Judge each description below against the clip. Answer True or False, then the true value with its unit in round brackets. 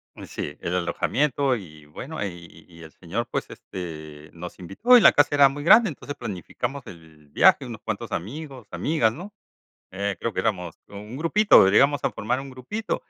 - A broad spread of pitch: True (8.6 semitones)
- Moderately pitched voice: False (110 Hz)